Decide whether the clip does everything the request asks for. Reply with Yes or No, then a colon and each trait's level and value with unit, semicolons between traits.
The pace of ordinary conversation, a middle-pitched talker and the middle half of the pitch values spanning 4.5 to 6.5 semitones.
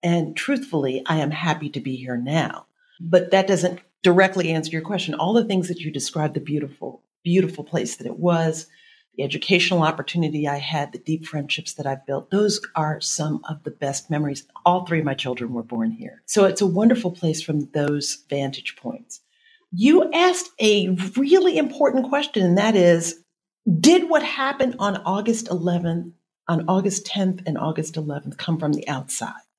Yes: average, 180 wpm; medium, 175 Hz; average, 5.1 semitones